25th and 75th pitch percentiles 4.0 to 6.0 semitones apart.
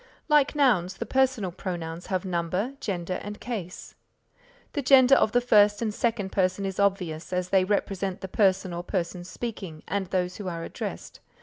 No: average, 3.1 semitones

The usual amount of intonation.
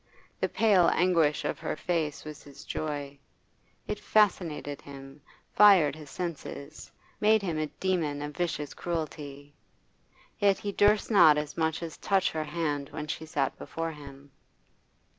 Yes: average, 3.5 semitones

